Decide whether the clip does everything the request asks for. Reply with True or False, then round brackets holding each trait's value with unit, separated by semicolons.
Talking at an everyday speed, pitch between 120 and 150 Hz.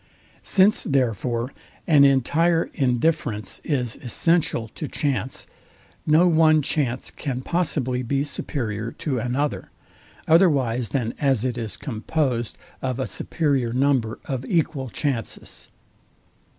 False (110 wpm; 135 Hz)